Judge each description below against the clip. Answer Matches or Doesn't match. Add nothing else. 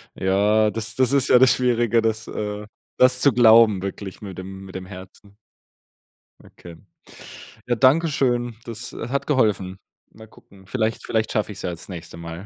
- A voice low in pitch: Matches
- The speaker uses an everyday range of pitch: Matches